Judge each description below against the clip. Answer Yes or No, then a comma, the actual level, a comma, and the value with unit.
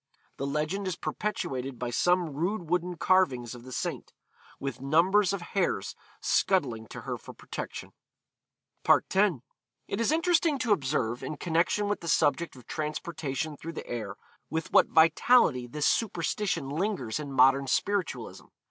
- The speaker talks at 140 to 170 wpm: Yes, average, 150 wpm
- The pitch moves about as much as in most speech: No, wide, 5.9 semitones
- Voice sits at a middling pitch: Yes, medium, 160 Hz